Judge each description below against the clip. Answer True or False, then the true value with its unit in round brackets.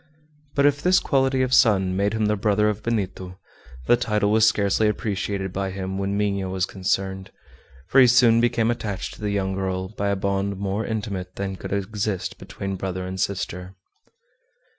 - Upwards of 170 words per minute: True (180 wpm)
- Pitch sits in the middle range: False (100 Hz)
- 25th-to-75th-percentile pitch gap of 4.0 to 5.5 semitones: False (2.4 semitones)